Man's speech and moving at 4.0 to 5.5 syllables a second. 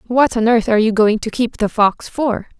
No: female; 5.1 syllables/s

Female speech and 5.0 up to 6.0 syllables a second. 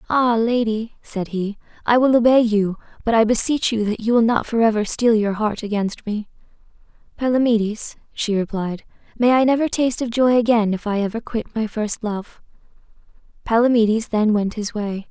Yes: female; 5.1 syllables/s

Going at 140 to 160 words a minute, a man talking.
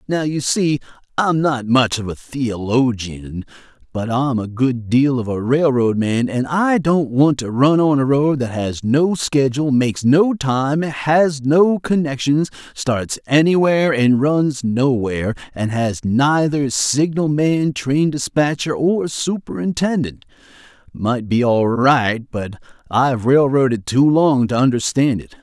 Yes: average, 150 wpm; male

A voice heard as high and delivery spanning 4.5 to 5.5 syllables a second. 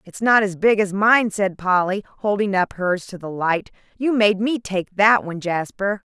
Yes: high, 200 Hz; 4.6 syllables/s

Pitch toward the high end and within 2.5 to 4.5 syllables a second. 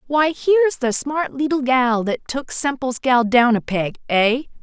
Yes: very high, 260 Hz; 4.4 syllables/s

